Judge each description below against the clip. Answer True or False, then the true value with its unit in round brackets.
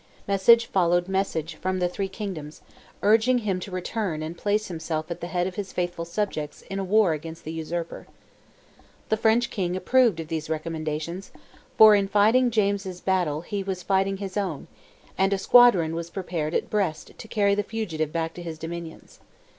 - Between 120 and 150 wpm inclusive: False (180 wpm)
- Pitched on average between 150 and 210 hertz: True (185 Hz)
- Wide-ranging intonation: False (3.7 semitones)